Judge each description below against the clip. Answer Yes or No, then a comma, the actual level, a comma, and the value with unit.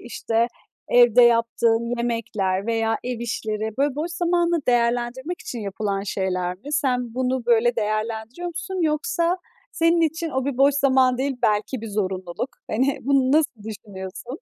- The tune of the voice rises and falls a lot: No, average, 4.2 semitones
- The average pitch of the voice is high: Yes, high, 240 Hz